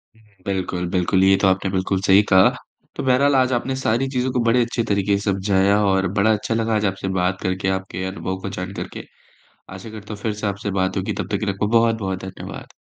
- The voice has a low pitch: Yes, low, 100 Hz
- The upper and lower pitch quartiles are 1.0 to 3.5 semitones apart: Yes, average, 2.8 semitones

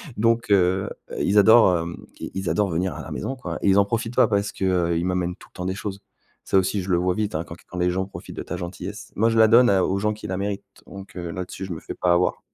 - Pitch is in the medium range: No, very low, 95 Hz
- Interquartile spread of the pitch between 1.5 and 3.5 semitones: Yes, narrow, 2.4 semitones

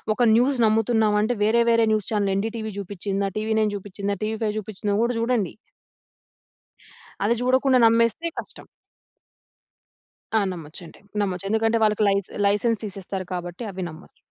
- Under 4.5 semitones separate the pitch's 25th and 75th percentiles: Yes, narrow, 2.6 semitones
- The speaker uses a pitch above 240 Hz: No, high, 215 Hz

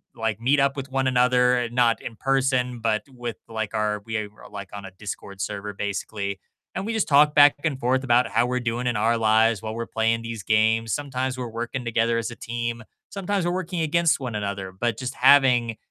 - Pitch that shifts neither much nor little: Yes, average, 3.1 semitones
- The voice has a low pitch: Yes, low, 120 Hz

